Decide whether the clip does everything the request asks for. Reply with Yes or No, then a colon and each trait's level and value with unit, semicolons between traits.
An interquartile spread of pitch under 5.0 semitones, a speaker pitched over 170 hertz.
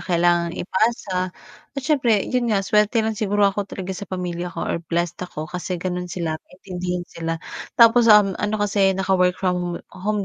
Yes: average, 2.9 semitones; high, 190 Hz